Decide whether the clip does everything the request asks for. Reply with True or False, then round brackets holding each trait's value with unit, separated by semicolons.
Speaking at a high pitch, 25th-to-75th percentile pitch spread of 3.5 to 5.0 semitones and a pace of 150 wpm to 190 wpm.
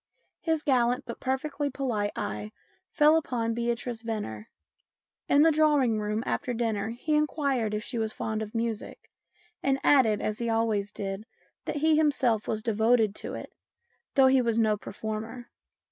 True (235 Hz; 3.9 semitones; 160 wpm)